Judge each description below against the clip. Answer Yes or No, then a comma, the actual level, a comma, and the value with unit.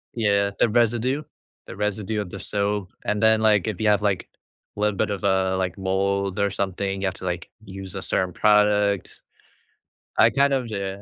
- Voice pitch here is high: No, low, 100 Hz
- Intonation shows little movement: Yes, narrow, 1.7 semitones